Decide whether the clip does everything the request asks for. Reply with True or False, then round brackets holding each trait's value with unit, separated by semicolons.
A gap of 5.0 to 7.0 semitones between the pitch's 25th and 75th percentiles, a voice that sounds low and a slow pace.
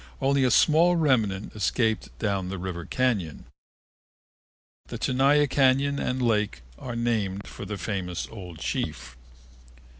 True (5.6 semitones; 110 Hz; 125 wpm)